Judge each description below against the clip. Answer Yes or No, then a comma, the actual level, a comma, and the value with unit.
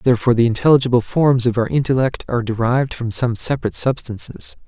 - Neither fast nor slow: Yes, average, 165 wpm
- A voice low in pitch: Yes, low, 125 Hz